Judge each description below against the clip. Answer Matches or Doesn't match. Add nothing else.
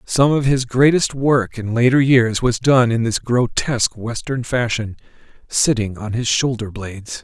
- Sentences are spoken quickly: Doesn't match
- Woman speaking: Doesn't match